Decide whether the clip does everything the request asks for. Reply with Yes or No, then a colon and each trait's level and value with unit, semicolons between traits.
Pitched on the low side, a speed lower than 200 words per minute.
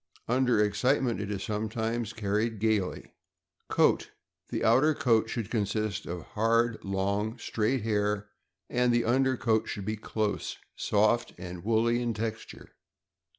Yes: low, 110 Hz; average, 140 wpm